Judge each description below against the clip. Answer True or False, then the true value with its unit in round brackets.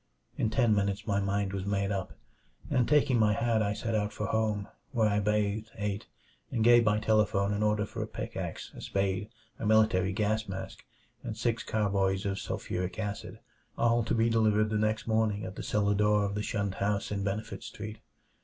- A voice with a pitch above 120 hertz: False (105 Hz)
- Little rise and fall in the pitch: True (1.6 semitones)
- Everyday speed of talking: True (195 wpm)